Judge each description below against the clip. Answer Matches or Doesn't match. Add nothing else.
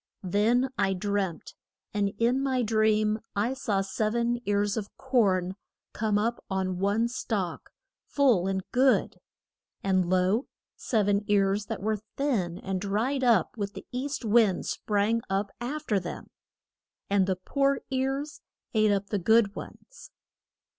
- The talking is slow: Doesn't match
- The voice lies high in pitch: Matches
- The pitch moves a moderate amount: Matches